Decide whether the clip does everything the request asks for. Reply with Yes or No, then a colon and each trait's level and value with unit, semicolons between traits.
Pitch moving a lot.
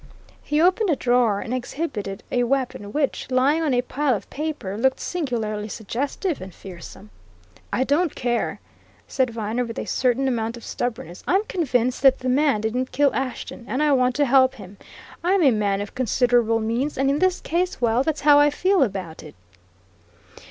No: average, 4.4 semitones